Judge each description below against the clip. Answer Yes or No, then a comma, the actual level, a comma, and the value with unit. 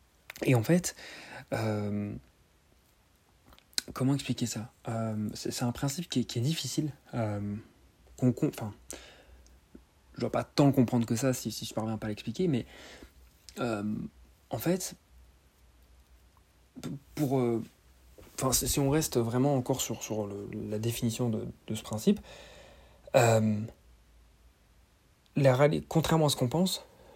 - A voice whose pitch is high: No, low, 115 Hz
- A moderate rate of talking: No, slow, 135 wpm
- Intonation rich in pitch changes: Yes, wide, 7.1 semitones